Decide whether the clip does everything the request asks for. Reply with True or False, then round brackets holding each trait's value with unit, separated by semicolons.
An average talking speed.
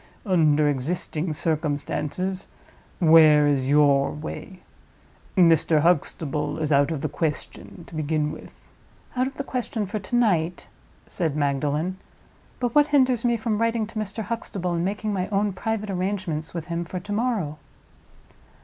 True (150 wpm)